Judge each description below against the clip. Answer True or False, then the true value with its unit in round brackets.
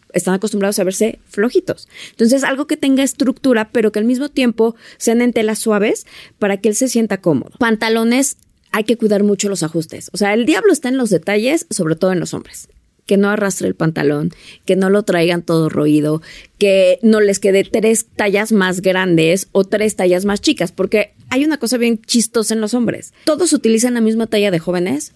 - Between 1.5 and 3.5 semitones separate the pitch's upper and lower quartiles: False (4.0 semitones)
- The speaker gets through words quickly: True (205 wpm)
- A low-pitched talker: False (215 Hz)